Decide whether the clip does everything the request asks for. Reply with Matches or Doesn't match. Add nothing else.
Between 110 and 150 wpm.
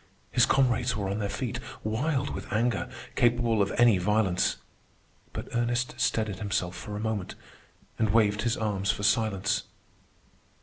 Matches